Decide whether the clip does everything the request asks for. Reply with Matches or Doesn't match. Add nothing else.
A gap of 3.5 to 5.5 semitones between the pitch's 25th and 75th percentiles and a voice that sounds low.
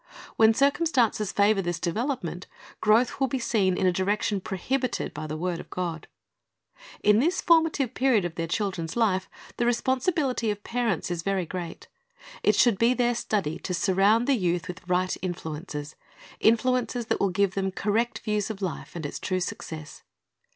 Doesn't match